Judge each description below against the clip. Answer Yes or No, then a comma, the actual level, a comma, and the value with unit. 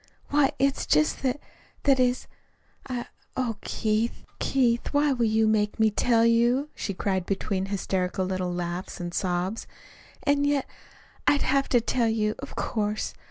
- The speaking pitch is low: No, high, 225 Hz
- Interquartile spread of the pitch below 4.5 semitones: No, average, 5.0 semitones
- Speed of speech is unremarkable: Yes, average, 155 wpm